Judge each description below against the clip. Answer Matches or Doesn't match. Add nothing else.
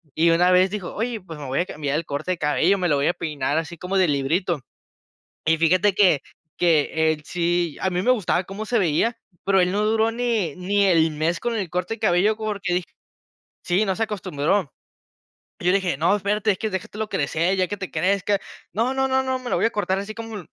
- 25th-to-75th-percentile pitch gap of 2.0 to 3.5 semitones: Doesn't match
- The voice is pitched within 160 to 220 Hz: Matches